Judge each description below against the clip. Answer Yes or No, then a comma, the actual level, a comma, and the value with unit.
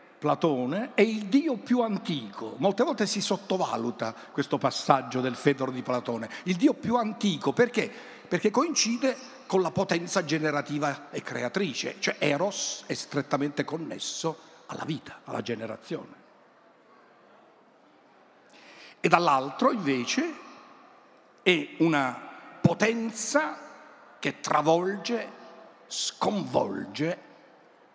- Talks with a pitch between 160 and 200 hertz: Yes, medium, 185 Hz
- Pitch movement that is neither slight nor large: No, wide, 8.3 semitones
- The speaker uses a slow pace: Yes, slow, 100 wpm